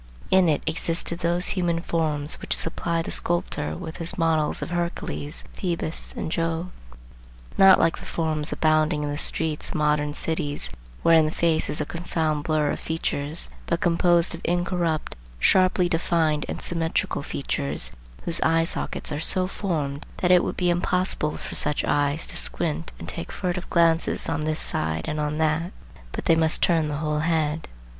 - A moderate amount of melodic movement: No, narrow, 2.1 semitones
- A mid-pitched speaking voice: Yes, medium, 165 Hz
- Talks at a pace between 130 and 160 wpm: No, average, 170 wpm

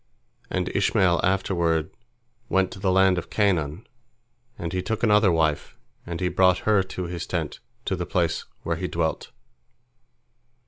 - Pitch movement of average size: No, narrow, 2.2 semitones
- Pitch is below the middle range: Yes, very low, 90 Hz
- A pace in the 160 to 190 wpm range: No, average, 150 wpm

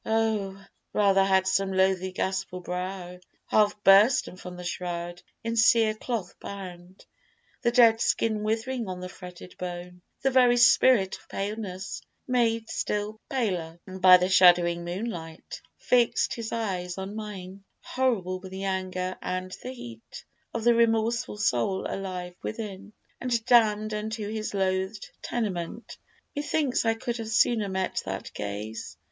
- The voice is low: No, high, 195 Hz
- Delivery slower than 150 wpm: Yes, average, 140 wpm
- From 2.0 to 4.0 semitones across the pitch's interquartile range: Yes, average, 3.6 semitones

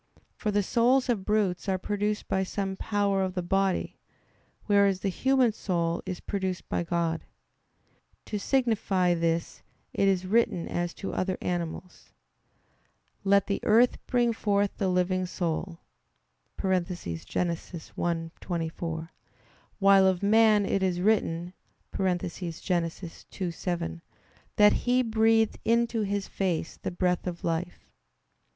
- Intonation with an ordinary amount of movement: Yes, average, 3.0 semitones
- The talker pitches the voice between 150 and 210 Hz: Yes, high, 190 Hz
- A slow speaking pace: Yes, slow, 125 wpm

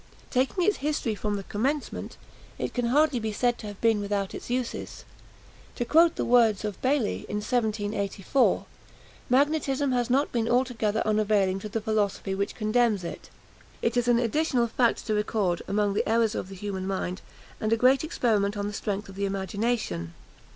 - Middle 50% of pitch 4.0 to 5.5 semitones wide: No, average, 3.4 semitones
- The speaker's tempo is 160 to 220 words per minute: Yes, average, 180 wpm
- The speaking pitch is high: Yes, high, 220 Hz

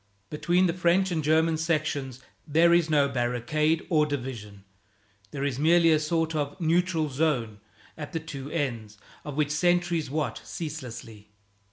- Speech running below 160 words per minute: Yes, average, 150 wpm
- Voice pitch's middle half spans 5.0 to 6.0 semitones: No, average, 3.5 semitones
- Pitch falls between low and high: Yes, medium, 155 Hz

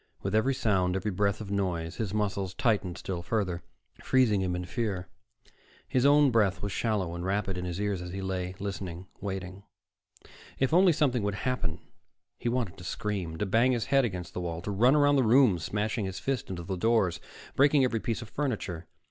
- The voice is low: Yes, low, 100 Hz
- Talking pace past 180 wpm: Yes, average, 195 wpm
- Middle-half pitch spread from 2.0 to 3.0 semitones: No, average, 4.5 semitones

